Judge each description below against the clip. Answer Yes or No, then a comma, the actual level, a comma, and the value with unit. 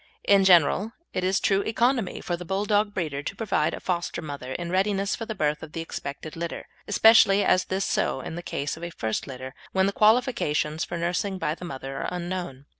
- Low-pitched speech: No, medium, 180 Hz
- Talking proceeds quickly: Yes, fast, 210 wpm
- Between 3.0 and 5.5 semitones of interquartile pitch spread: Yes, average, 4.5 semitones